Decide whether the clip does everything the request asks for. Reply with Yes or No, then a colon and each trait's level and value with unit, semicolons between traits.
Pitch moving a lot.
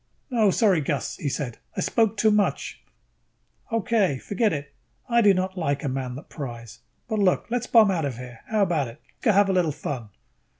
Yes: wide, 7.2 semitones